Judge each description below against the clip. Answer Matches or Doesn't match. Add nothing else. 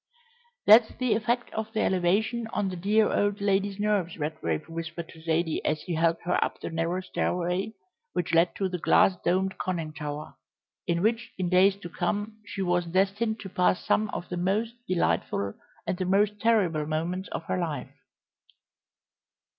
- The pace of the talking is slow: Doesn't match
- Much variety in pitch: Doesn't match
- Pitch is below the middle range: Doesn't match